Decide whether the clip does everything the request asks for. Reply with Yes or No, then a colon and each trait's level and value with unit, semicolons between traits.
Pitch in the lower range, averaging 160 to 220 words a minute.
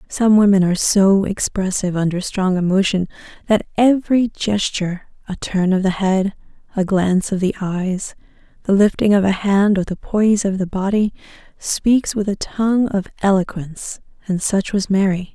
No: high, 195 Hz; average, 165 wpm